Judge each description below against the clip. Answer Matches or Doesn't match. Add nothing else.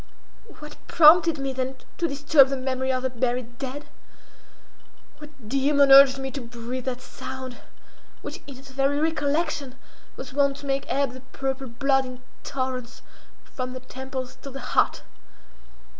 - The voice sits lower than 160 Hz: Doesn't match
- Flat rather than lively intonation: Matches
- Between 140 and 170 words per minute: Matches